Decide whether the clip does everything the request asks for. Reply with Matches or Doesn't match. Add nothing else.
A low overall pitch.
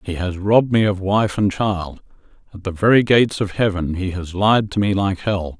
Matches